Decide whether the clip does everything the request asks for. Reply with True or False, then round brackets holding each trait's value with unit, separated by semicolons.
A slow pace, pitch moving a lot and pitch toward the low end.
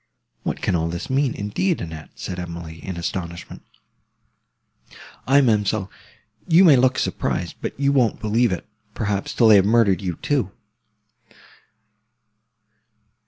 True (130 wpm; 6.7 semitones; 105 Hz)